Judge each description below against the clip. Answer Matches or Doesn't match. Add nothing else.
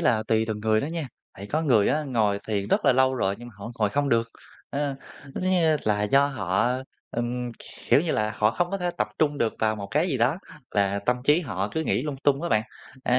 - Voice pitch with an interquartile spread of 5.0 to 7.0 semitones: Matches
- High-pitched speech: Doesn't match